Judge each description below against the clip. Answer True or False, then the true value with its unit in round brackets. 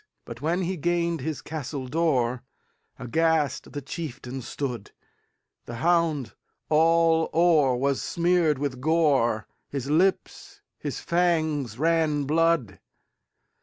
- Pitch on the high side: False (155 Hz)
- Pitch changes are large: False (4.2 semitones)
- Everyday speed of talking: False (95 wpm)